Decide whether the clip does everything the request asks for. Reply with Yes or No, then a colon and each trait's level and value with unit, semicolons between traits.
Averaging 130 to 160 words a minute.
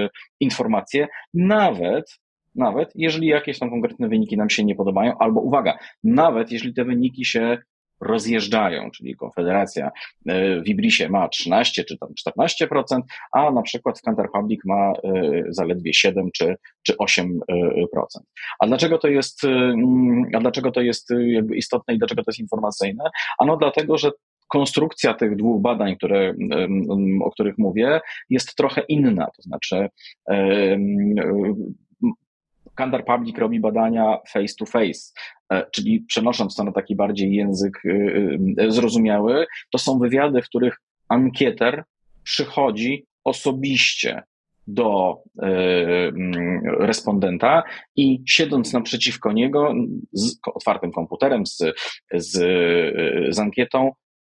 No: average, 120 wpm